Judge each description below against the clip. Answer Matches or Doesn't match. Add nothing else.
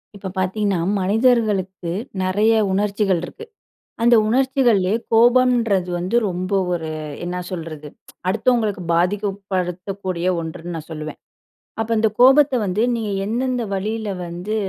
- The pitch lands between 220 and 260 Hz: Doesn't match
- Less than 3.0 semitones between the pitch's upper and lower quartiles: Doesn't match